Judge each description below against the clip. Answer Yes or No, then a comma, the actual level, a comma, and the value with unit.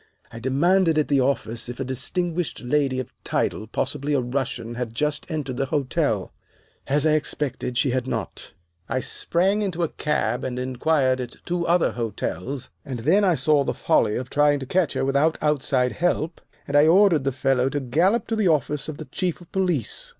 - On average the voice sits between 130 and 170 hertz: Yes, medium, 140 Hz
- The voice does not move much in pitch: No, average, 4.0 semitones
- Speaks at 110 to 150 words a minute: No, average, 195 wpm